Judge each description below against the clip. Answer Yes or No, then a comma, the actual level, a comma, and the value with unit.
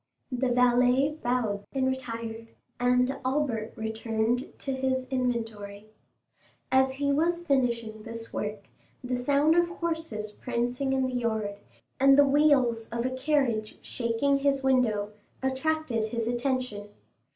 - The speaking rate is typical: No, slow, 130 wpm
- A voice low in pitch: No, very high, 250 Hz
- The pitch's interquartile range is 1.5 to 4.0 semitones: Yes, average, 3.1 semitones